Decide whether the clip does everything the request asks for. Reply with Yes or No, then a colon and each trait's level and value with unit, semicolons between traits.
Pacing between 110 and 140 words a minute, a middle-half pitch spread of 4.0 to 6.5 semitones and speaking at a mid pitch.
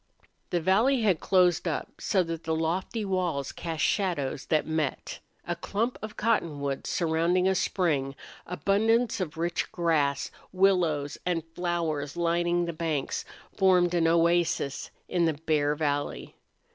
No: slow, 135 wpm; average, 2.9 semitones; medium, 170 Hz